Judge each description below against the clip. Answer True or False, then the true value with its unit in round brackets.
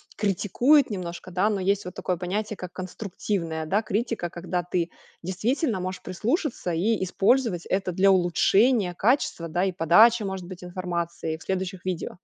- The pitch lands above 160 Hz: True (185 Hz)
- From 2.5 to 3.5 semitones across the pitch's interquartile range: True (3.1 semitones)